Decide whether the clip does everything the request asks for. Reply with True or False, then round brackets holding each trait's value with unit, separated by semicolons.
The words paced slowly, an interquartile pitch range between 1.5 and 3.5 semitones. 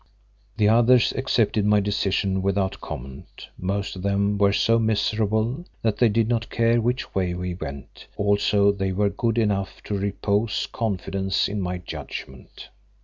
False (150 wpm; 2.5 semitones)